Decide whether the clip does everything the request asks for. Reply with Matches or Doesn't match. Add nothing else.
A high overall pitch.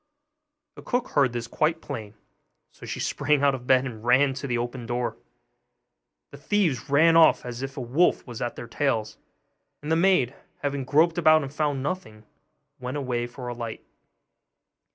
Doesn't match